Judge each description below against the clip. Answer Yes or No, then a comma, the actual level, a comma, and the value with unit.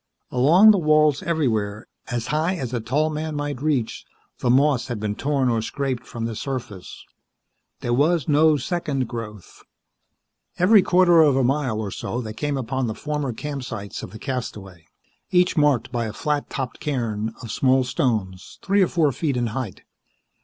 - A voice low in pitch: Yes, low, 130 Hz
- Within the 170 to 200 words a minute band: Yes, average, 175 wpm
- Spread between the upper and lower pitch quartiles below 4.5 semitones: No, average, 4.8 semitones